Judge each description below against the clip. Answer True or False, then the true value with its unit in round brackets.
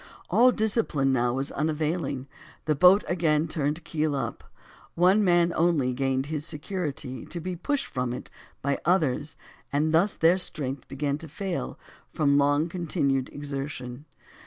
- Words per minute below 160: True (145 wpm)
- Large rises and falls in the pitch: False (3.8 semitones)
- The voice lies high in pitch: False (150 Hz)